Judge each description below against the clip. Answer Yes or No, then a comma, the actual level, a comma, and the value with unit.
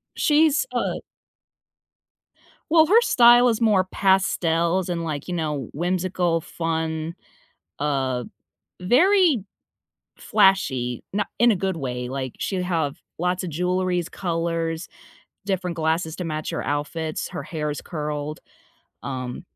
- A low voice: No, medium, 170 Hz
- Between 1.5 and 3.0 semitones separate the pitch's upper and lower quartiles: No, average, 3.8 semitones